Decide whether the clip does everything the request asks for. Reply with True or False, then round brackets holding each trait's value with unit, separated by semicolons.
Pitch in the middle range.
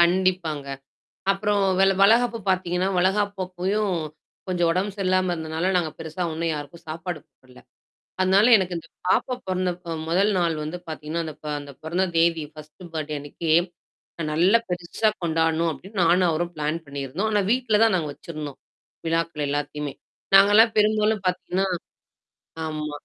True (175 Hz)